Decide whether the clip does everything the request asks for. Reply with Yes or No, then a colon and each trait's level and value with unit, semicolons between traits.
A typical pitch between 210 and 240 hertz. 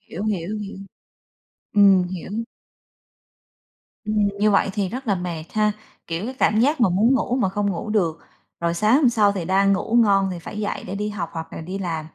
No: high, 200 Hz